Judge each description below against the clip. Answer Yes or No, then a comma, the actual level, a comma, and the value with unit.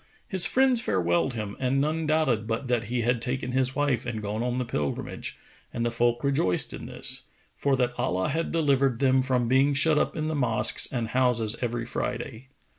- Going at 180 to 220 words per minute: Yes, average, 195 wpm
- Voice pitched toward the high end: No, low, 125 Hz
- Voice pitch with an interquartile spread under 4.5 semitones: Yes, average, 3.2 semitones